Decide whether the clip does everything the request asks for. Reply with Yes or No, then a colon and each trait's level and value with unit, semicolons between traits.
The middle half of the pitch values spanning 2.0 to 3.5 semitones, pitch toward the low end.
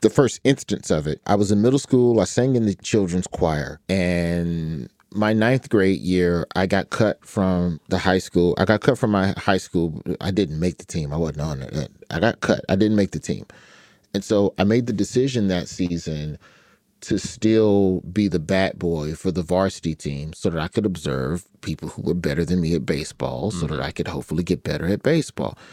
No: average, 4.0 semitones; very low, 90 Hz